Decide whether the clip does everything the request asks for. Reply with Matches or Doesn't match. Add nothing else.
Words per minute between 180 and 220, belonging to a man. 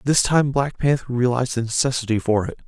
Matches